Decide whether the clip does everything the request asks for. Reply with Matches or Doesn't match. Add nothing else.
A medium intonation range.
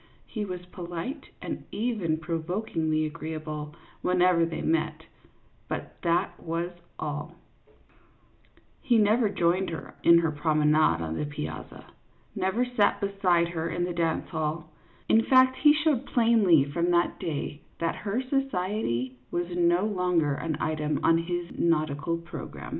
Matches